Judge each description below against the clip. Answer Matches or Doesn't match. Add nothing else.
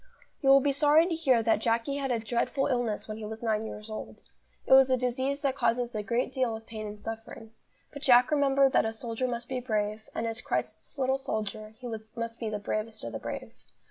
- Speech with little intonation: Doesn't match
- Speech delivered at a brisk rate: Matches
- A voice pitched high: Matches